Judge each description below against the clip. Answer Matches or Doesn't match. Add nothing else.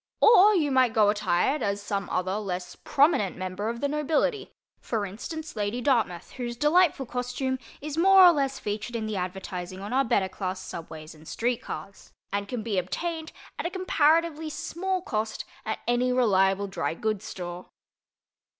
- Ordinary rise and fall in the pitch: Doesn't match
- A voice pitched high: Matches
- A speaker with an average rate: Matches